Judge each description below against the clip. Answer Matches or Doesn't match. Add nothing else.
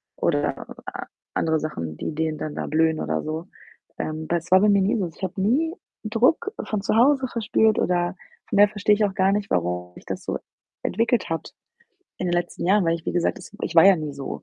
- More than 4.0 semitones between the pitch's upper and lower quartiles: Matches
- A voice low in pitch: Doesn't match